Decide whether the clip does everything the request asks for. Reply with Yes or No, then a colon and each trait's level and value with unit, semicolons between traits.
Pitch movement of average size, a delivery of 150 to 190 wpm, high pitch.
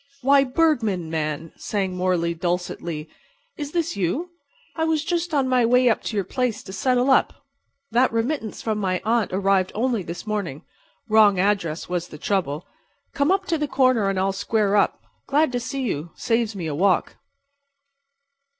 No: wide, 6.1 semitones; average, 170 wpm; high, 215 Hz